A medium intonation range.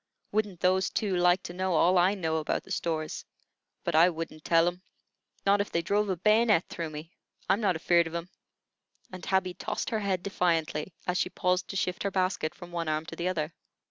No: narrow, 2.3 semitones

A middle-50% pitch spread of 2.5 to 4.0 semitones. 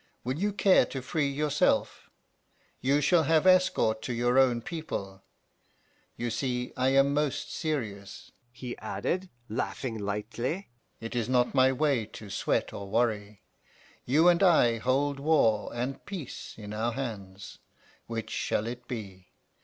No: average, 4.6 semitones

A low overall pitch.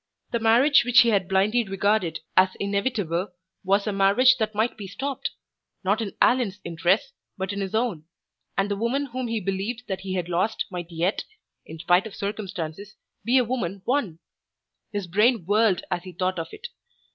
No: high, 200 Hz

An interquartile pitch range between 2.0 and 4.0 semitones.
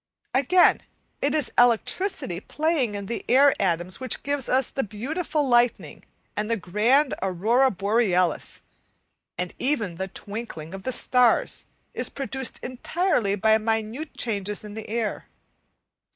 No: average, 4.8 semitones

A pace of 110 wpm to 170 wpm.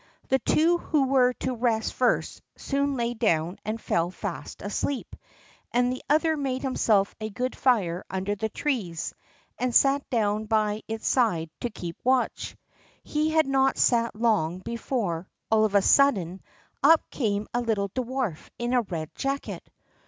Yes: average, 160 wpm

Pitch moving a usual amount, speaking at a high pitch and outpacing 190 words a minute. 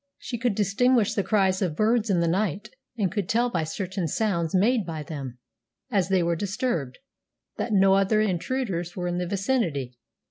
No: average, 4.0 semitones; high, 195 Hz; average, 180 wpm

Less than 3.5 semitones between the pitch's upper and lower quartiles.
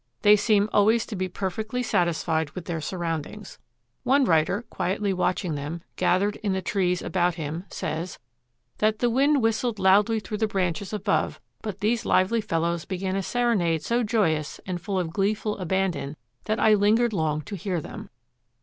No: average, 3.9 semitones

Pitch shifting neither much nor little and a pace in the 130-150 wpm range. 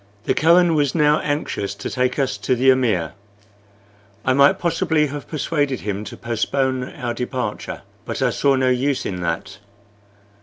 No: average, 3.5 semitones; average, 160 wpm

